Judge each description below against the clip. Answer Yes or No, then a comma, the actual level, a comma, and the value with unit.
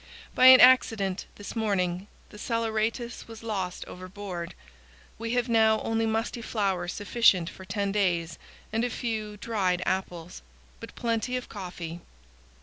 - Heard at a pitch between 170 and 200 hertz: No, high, 210 Hz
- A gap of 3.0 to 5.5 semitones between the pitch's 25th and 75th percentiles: Yes, average, 3.7 semitones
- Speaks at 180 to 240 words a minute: No, average, 140 wpm